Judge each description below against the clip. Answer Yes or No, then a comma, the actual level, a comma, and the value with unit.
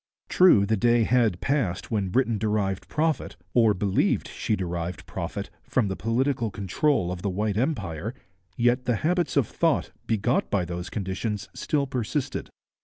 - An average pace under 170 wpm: Yes, average, 155 wpm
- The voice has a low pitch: Yes, low, 110 Hz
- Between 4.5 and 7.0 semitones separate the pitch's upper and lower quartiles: Yes, average, 4.8 semitones